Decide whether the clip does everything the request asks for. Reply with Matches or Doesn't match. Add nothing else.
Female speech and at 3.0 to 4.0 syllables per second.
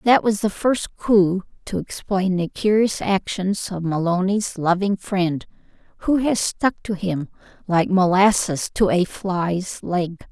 Matches